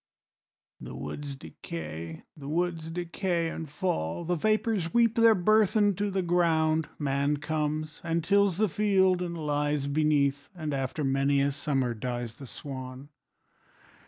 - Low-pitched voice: No, medium, 155 Hz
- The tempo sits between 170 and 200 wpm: No, average, 145 wpm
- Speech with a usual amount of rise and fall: Yes, average, 4.3 semitones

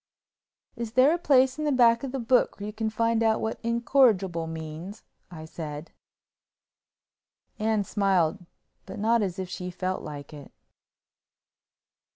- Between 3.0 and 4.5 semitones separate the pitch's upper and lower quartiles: No, average, 5.0 semitones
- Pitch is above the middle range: Yes, high, 210 Hz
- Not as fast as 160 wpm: Yes, average, 150 wpm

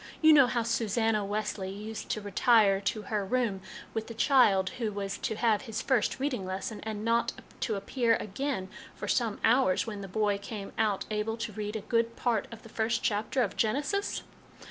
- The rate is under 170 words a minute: No, average, 190 wpm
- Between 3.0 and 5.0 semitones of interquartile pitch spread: No, narrow, 2.4 semitones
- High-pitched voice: Yes, high, 220 Hz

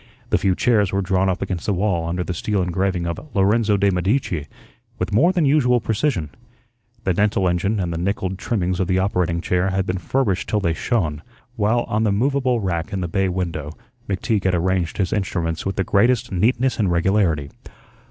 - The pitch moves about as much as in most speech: Yes, average, 3.2 semitones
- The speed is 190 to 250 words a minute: Yes, average, 195 wpm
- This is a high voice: No, very low, 95 Hz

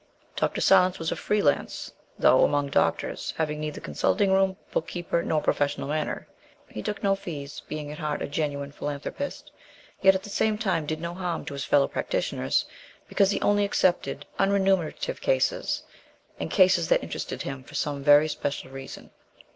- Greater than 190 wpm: No, average, 170 wpm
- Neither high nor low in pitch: Yes, medium, 160 Hz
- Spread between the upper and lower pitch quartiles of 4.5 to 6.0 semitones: Yes, average, 4.9 semitones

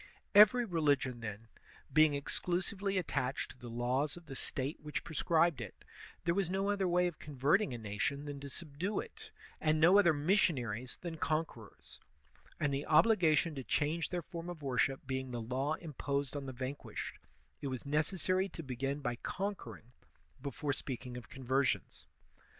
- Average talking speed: Yes, average, 160 wpm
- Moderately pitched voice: Yes, medium, 145 Hz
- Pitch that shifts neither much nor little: Yes, average, 4.8 semitones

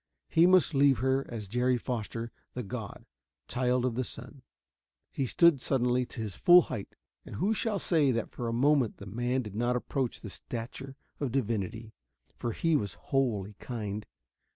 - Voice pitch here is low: Yes, low, 125 Hz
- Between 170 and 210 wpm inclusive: Yes, average, 175 wpm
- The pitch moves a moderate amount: Yes, average, 3.1 semitones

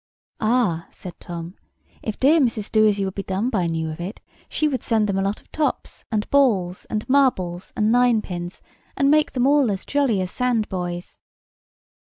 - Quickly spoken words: No, average, 165 wpm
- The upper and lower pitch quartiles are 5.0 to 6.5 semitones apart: Yes, wide, 5.5 semitones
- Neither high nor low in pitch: No, high, 215 Hz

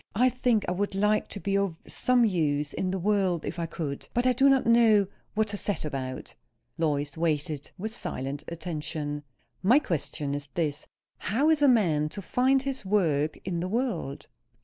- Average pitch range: No, wide, 6.7 semitones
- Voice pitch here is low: No, medium, 185 Hz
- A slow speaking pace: No, average, 185 wpm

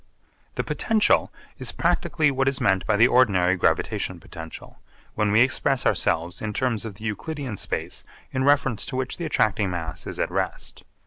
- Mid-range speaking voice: No, low, 110 Hz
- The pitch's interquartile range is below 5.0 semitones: No, wide, 5.6 semitones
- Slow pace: No, average, 175 wpm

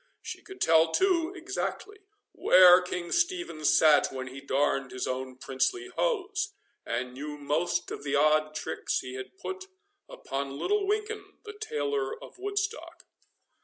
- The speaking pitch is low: No, medium, 170 Hz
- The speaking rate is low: No, average, 145 wpm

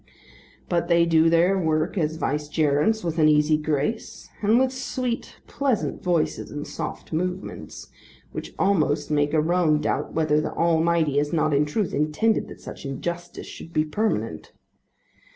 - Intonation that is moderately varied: Yes, average, 3.1 semitones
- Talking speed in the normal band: Yes, average, 150 wpm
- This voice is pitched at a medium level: Yes, medium, 160 Hz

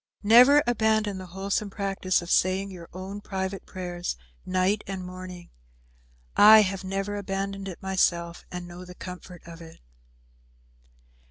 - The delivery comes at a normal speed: Yes, average, 145 wpm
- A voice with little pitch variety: Yes, narrow, 1.6 semitones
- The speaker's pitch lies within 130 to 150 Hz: No, high, 190 Hz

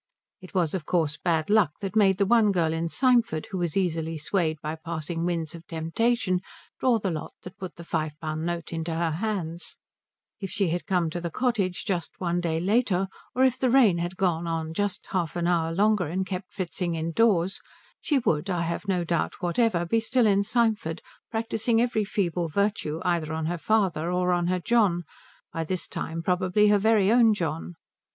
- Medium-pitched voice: Yes, medium, 180 Hz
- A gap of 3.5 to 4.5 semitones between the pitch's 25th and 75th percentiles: Yes, average, 3.9 semitones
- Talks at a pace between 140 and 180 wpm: No, average, 195 wpm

